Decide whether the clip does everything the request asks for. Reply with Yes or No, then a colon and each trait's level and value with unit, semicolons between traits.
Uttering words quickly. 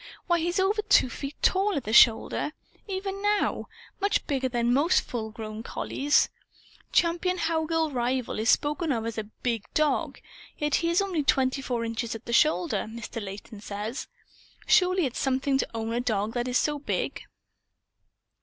No: average, 170 wpm